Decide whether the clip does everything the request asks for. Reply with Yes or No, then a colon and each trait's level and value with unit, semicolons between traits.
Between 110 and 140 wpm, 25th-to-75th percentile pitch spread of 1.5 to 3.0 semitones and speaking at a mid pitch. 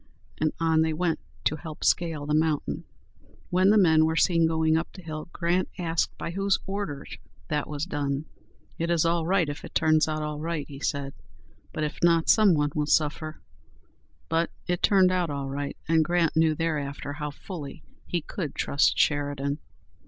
No: average, 180 wpm; narrow, 2.4 semitones; medium, 160 Hz